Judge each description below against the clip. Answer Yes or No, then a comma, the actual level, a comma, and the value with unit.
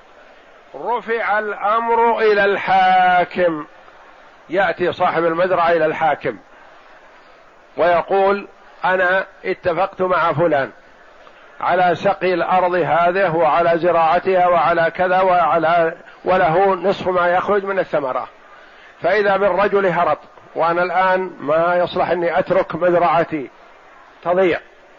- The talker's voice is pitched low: No, medium, 180 Hz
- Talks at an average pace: Yes, average, 95 wpm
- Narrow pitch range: Yes, narrow, 2.0 semitones